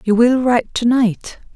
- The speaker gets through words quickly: No, average, 195 wpm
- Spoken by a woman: Yes, female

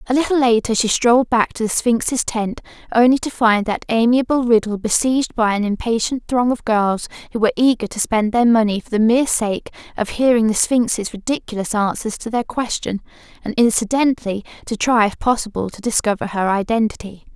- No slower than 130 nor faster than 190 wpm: Yes, average, 185 wpm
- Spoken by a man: No, female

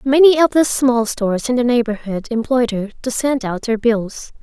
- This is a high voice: Yes, high, 240 Hz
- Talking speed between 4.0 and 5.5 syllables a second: Yes, 4.8 syllables/s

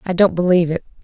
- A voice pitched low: No, medium, 175 Hz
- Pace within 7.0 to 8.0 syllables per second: Yes, 7.8 syllables/s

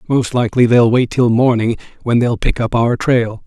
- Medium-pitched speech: No, low, 120 Hz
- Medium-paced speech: No, fast, 210 wpm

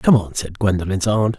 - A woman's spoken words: No, male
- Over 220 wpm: No, fast, 215 wpm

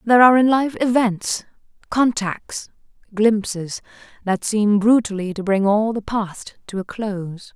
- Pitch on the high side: Yes, high, 215 Hz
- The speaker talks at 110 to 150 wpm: Yes, average, 145 wpm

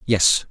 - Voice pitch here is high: No, low, 105 Hz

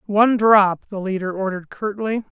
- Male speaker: Yes, male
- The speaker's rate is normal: Yes, average, 150 wpm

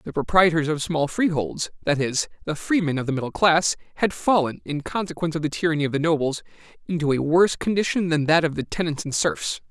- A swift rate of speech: Yes, fast, 210 wpm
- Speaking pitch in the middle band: Yes, medium, 160 Hz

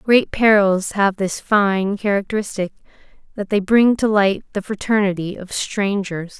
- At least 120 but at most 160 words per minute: Yes, average, 140 wpm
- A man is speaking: No, female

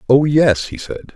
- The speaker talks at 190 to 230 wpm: Yes, fast, 205 wpm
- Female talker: No, male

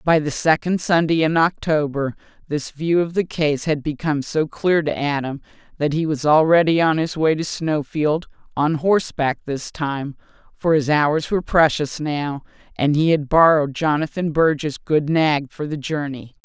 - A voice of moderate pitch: Yes, medium, 155 Hz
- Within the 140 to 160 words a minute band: No, average, 170 wpm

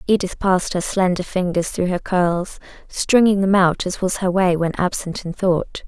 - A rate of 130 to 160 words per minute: No, average, 195 wpm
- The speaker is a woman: Yes, female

